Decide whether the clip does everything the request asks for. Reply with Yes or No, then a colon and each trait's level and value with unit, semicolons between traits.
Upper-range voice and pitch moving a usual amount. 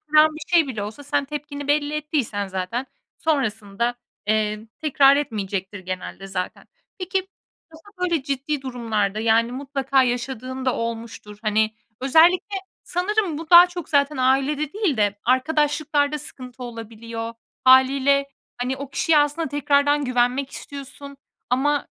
Yes: very high, 270 Hz; average, 4.3 semitones